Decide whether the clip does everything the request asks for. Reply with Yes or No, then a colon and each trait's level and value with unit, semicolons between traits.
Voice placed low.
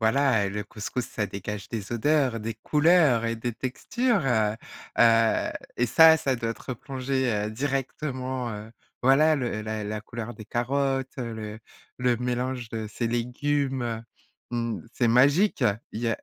Yes: low, 120 Hz